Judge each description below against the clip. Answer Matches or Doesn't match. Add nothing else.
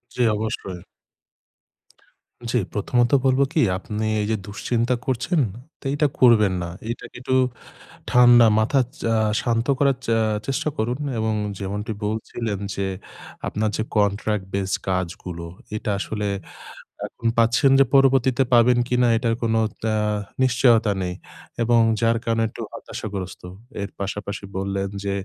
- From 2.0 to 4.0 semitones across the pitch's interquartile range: Matches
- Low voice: Matches